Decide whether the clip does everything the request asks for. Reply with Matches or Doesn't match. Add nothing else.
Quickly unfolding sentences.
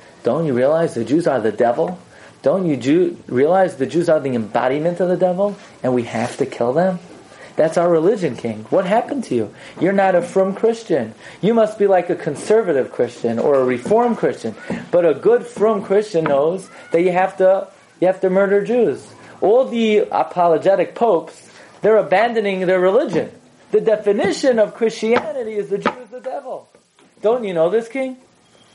Doesn't match